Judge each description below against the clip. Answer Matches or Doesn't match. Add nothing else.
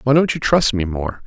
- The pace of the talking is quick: Matches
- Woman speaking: Doesn't match